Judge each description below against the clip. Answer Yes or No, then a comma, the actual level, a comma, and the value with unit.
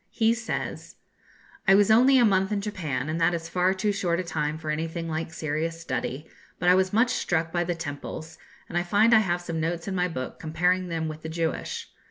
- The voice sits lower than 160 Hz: No, medium, 170 Hz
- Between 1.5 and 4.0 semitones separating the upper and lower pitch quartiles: Yes, average, 3.0 semitones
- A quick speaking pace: Yes, fast, 225 wpm